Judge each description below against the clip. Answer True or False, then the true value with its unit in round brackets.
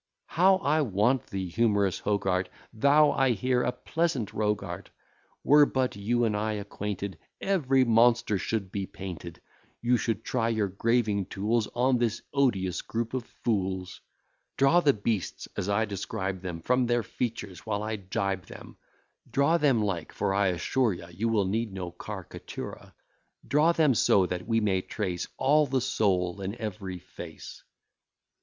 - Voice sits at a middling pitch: False (110 Hz)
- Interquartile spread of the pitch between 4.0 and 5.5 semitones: True (4.4 semitones)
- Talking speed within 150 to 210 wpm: True (160 wpm)